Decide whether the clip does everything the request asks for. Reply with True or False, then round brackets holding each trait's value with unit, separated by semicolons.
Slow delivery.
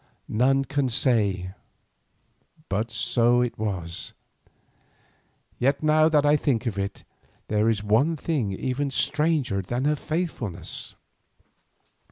True (115 wpm)